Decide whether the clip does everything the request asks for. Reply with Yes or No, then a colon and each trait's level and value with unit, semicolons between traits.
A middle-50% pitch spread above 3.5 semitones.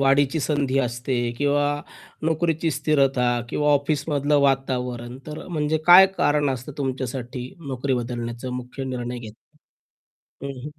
No: average, 2.9 semitones